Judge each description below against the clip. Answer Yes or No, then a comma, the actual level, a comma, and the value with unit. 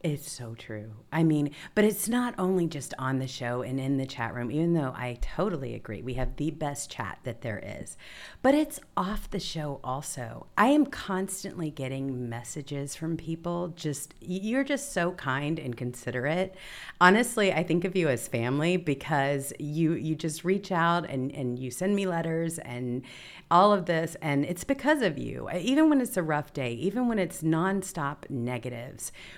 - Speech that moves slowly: No, average, 185 wpm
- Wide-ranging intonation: Yes, wide, 5.9 semitones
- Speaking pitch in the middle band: Yes, medium, 160 Hz